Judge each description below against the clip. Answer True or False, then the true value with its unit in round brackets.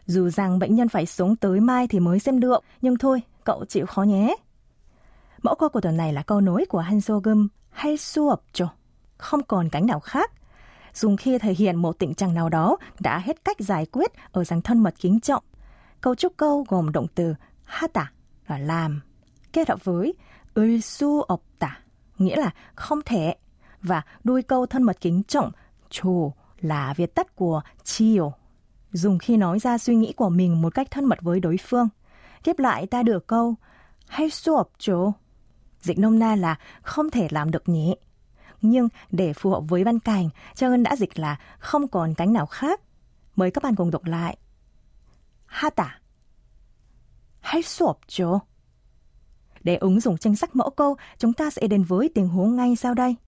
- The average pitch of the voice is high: True (200 Hz)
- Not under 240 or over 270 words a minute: False (185 wpm)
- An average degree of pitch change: False (6.2 semitones)